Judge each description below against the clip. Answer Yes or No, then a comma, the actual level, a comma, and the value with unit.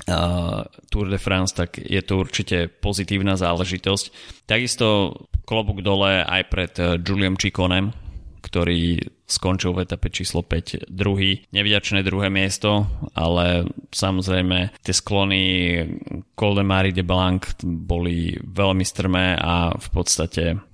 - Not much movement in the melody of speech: Yes, narrow, 2.1 semitones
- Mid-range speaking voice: No, very low, 95 Hz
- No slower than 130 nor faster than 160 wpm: No, average, 120 wpm